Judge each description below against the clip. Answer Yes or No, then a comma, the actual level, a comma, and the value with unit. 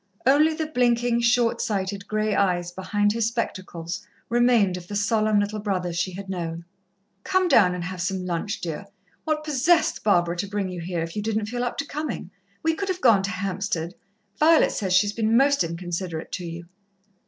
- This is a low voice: No, high, 205 Hz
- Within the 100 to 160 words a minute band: No, average, 190 wpm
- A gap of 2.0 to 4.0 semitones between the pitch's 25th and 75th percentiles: No, average, 4.8 semitones